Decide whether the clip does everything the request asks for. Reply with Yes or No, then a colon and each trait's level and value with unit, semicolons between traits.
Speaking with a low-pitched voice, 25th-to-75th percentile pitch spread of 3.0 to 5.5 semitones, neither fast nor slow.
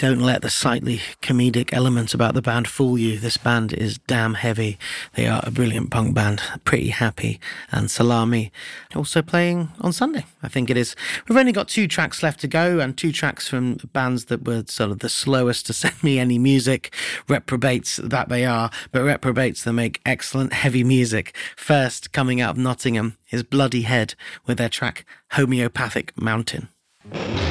No: low, 125 Hz; narrow, 2.6 semitones; average, 180 wpm